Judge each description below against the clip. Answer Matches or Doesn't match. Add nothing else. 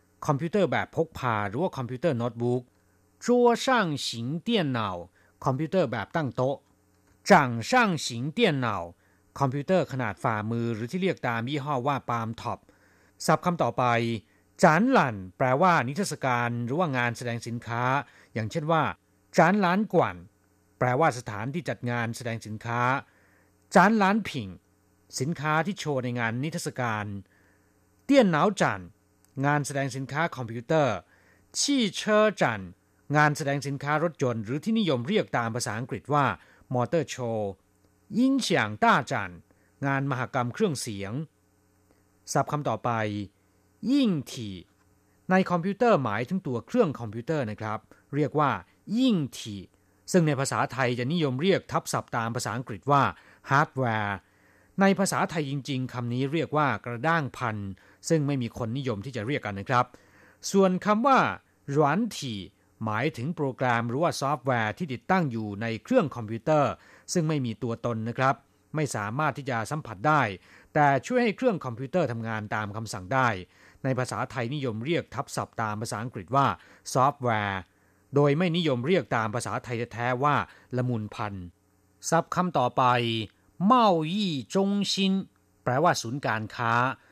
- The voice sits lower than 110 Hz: Doesn't match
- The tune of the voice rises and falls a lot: Matches